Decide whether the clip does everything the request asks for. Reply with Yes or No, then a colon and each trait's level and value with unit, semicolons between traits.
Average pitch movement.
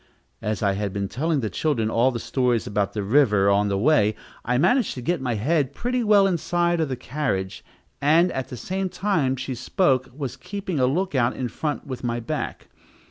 No: wide, 6.3 semitones